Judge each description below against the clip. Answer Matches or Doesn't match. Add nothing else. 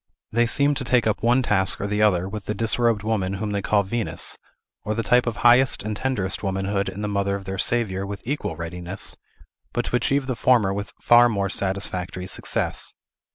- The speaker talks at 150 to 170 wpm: Doesn't match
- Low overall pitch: Matches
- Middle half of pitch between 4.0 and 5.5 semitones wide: Doesn't match